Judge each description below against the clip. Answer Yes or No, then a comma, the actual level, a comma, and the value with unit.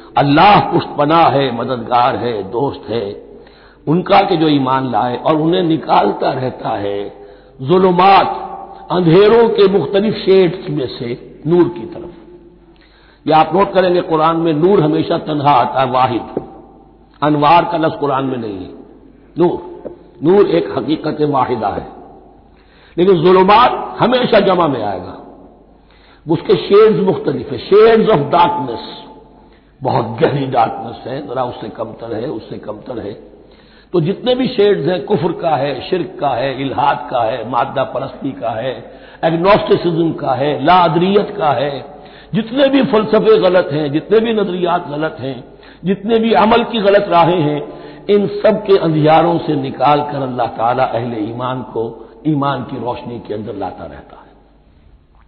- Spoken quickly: No, average, 150 wpm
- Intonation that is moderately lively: No, wide, 6.6 semitones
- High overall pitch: No, medium, 165 Hz